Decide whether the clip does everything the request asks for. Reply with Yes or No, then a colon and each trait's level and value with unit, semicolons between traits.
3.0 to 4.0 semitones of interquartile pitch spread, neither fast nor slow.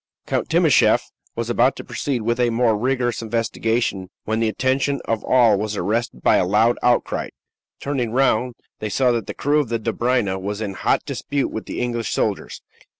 No: narrow, 2.5 semitones; average, 185 wpm